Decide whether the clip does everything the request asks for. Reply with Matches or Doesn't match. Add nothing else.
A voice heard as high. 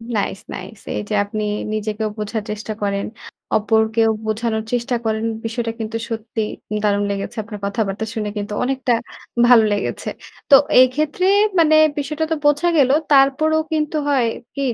Matches